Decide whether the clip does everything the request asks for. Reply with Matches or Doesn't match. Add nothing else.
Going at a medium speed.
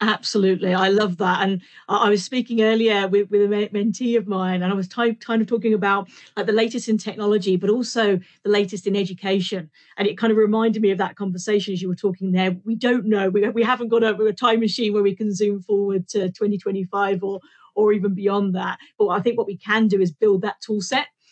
Doesn't match